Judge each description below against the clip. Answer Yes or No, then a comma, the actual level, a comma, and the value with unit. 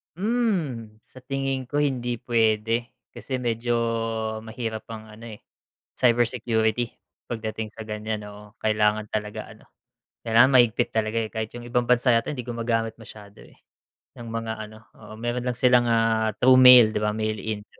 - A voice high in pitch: No, low, 115 Hz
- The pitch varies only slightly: Yes, narrow, 2.1 semitones